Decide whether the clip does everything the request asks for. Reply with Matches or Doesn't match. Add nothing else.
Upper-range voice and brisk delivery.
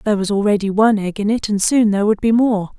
Matches